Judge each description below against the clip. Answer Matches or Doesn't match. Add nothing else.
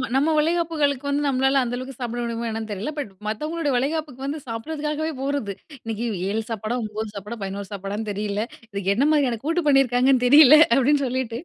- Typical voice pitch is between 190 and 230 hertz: Doesn't match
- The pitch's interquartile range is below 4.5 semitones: Doesn't match